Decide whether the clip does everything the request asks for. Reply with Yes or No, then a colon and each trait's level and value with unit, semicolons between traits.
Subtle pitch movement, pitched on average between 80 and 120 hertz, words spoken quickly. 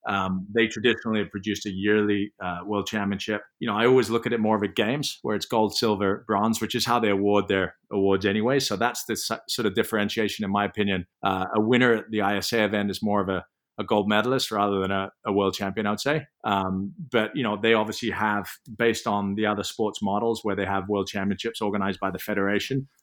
Yes: narrow, 2.1 semitones; low, 105 Hz; fast, 230 wpm